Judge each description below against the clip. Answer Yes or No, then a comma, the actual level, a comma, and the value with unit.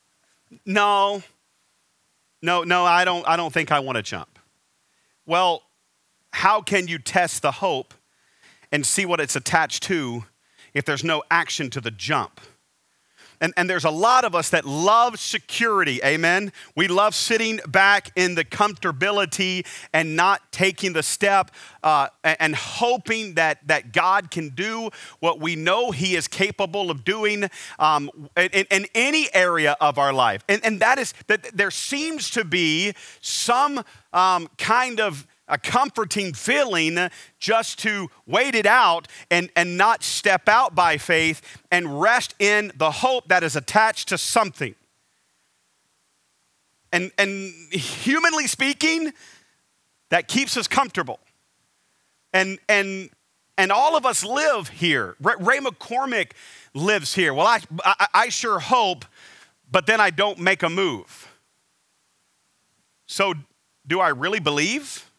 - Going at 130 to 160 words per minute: Yes, average, 145 wpm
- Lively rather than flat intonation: No, average, 4.5 semitones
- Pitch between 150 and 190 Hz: Yes, medium, 185 Hz